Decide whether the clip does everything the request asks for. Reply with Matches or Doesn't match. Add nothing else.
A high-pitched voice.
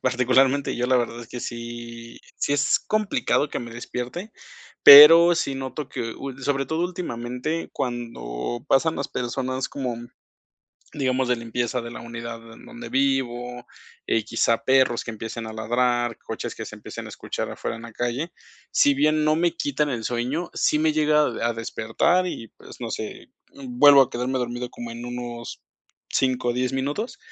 Doesn't match